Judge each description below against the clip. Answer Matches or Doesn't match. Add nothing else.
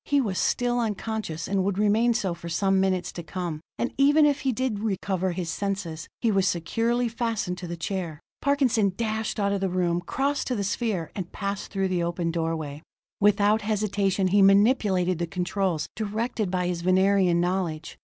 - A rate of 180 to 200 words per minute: Matches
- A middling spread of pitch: Matches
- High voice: Matches